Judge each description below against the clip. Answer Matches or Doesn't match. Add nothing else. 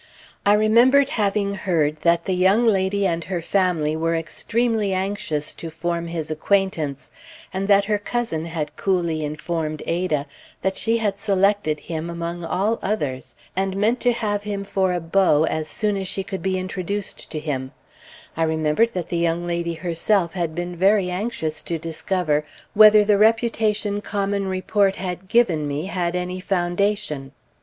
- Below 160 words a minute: Doesn't match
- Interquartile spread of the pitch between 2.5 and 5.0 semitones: Matches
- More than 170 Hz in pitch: Matches